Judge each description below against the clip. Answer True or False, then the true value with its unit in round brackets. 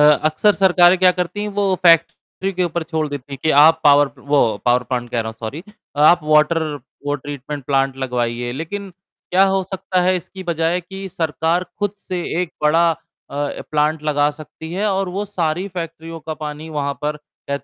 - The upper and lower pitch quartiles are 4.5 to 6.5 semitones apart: False (3.7 semitones)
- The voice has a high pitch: False (160 Hz)